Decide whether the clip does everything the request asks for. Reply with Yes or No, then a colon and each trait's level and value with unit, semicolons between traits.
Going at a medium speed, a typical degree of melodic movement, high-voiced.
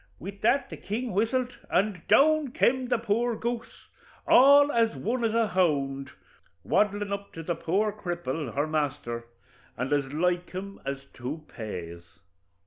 No: average, 150 wpm; wide, 8.1 semitones; high, 195 Hz